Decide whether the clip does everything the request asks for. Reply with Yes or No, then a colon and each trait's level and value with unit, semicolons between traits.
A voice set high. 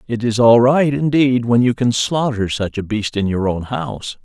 No: low, 120 Hz